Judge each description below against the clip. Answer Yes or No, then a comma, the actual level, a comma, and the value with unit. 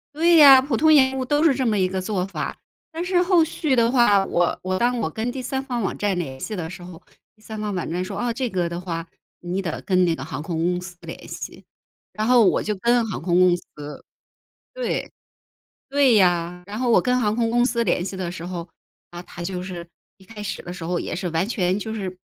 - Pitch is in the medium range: No, high, 200 Hz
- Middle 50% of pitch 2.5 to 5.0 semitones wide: No, wide, 5.5 semitones